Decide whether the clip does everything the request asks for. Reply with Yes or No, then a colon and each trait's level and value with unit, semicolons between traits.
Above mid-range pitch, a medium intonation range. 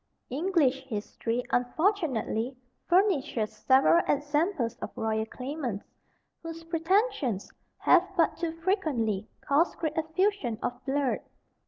No: very high, 290 Hz; wide, 5.7 semitones